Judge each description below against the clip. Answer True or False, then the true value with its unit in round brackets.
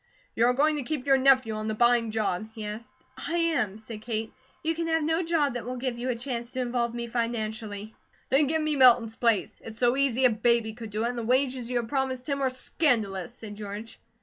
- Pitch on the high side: True (240 Hz)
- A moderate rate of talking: False (235 wpm)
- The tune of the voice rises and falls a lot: False (3.2 semitones)